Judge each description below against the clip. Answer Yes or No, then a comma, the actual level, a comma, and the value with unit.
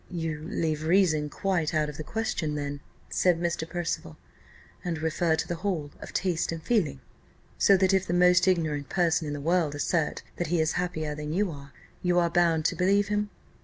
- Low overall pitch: No, medium, 165 Hz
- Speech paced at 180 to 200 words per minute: Yes, average, 195 wpm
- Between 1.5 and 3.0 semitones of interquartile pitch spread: Yes, average, 2.7 semitones